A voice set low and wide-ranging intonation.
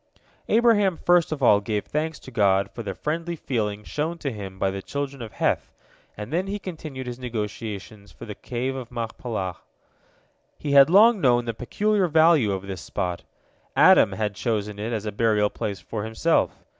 Yes: low, 120 Hz; wide, 6.9 semitones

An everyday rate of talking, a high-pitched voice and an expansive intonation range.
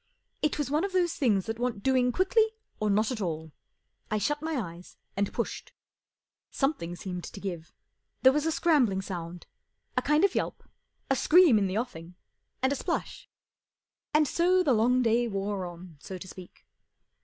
Yes: average, 180 wpm; high, 230 Hz; wide, 8.0 semitones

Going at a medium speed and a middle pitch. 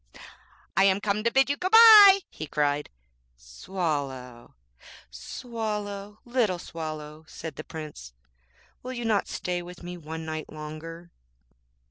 No: slow, 125 wpm; medium, 170 Hz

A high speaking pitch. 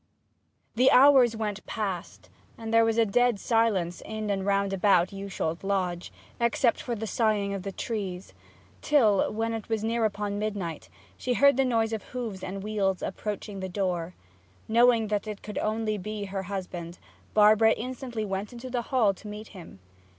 Yes: high, 210 Hz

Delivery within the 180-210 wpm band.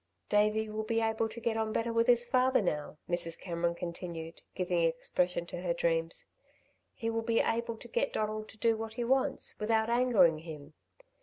Yes: average, 185 wpm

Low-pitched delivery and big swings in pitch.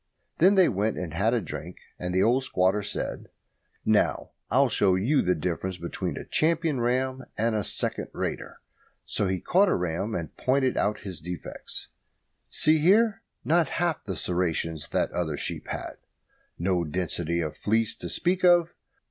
Yes: low, 105 Hz; wide, 7.7 semitones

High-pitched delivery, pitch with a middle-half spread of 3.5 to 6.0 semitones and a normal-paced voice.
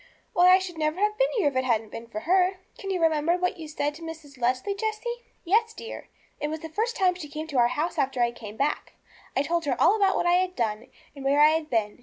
No: very high, 320 Hz; wide, 5.5 semitones; fast, 265 wpm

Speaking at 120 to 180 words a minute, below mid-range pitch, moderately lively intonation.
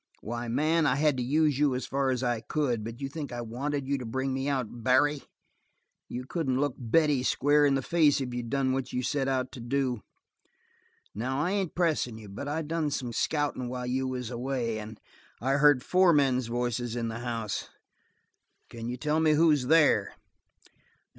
No: average, 195 wpm; low, 130 Hz; average, 3.3 semitones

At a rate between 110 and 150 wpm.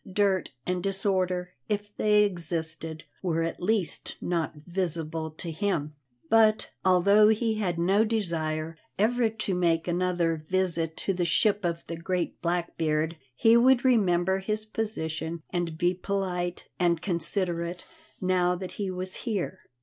Yes: average, 140 wpm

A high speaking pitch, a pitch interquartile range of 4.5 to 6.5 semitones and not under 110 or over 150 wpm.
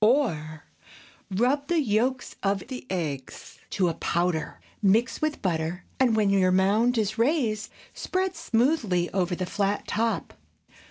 Yes: high, 210 Hz; wide, 5.5 semitones; average, 140 wpm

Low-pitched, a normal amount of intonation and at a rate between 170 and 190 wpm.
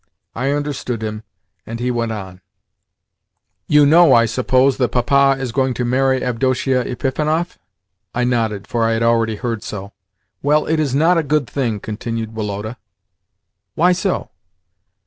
No: low, 125 Hz; average, 3.4 semitones; average, 150 wpm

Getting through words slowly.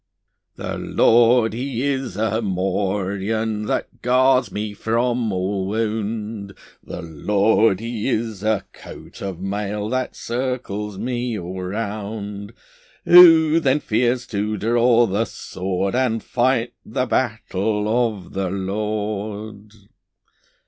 Yes: slow, 115 wpm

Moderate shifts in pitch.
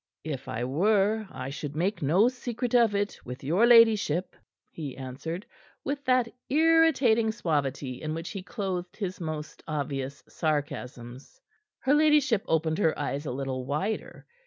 No: wide, 7.8 semitones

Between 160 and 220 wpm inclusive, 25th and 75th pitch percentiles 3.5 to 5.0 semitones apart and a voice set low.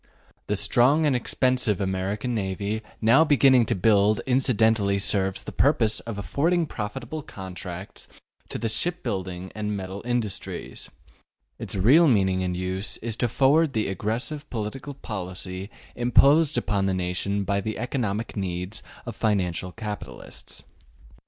No: average, 140 wpm; average, 4.5 semitones; low, 105 Hz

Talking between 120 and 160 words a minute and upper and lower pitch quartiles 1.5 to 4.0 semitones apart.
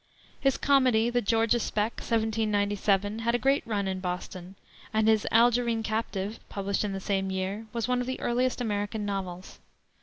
No: average, 170 wpm; average, 2.9 semitones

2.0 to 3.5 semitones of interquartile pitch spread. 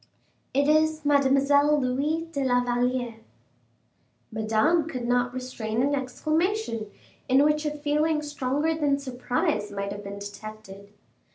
No: average, 4.6 semitones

